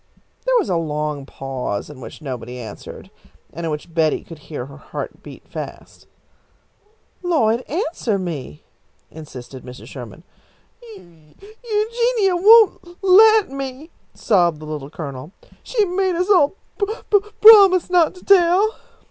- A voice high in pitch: Yes, high, 240 Hz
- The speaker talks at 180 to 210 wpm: No, average, 140 wpm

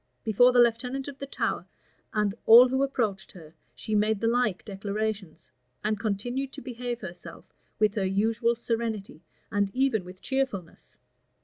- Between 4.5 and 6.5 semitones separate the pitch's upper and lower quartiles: No, average, 3.6 semitones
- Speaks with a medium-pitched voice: No, high, 220 Hz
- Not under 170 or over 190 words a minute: No, average, 150 wpm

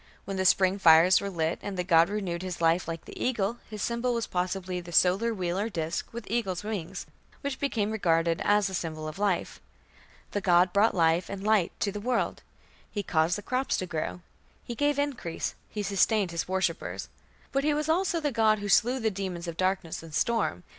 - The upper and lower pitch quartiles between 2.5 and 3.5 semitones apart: No, average, 4.2 semitones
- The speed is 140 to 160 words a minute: No, fast, 205 wpm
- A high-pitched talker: Yes, high, 195 Hz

